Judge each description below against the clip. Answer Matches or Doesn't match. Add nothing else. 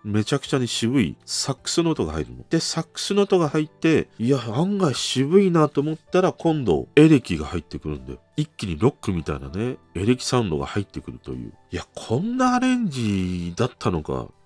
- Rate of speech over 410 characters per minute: Doesn't match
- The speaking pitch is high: Doesn't match